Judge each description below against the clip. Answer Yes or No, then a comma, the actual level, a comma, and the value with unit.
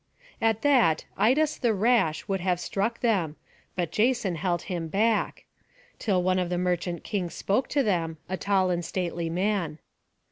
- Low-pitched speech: No, medium, 185 Hz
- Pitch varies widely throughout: No, average, 4.1 semitones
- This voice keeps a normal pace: Yes, average, 165 wpm